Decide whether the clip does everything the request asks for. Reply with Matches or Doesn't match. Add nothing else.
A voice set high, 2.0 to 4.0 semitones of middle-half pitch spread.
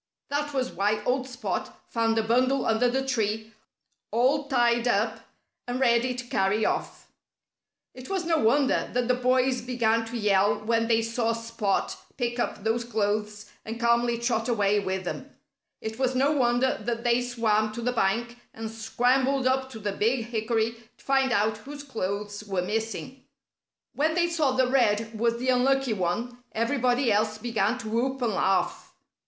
Matches